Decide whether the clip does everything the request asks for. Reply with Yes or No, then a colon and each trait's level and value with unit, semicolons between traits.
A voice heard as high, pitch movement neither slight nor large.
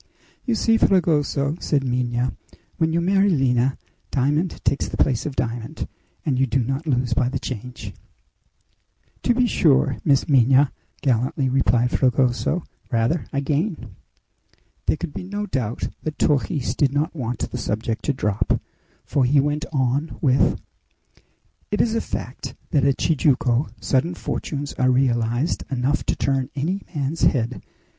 No: low, 135 Hz; average, 3.7 semitones